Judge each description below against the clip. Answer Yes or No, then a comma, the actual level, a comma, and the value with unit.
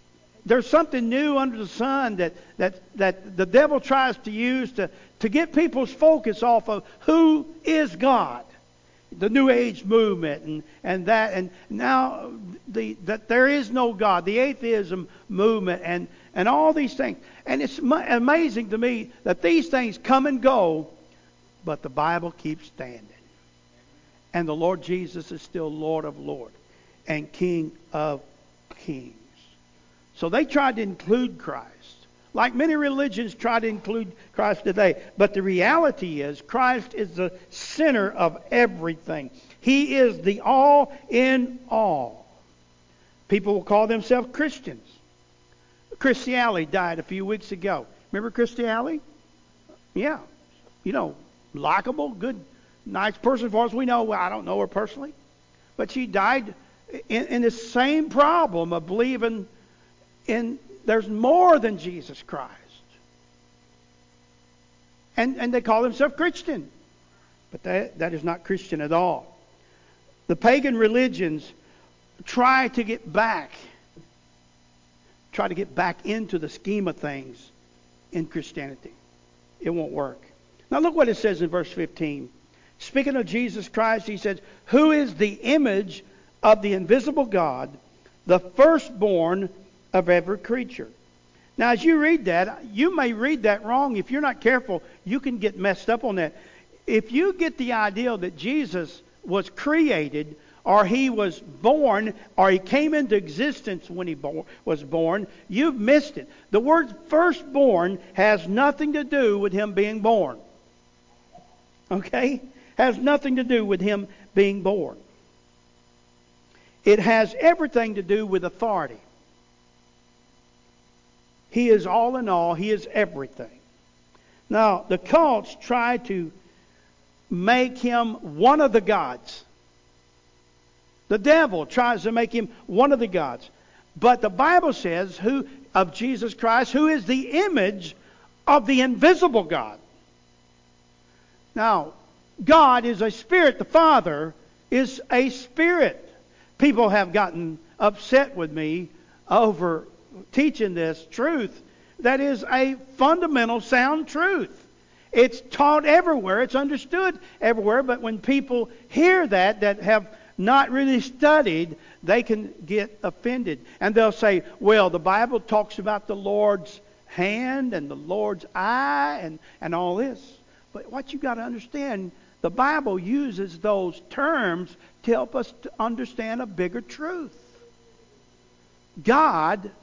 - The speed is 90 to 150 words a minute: Yes, average, 140 wpm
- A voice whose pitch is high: Yes, high, 210 Hz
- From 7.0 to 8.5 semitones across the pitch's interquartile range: Yes, wide, 7.9 semitones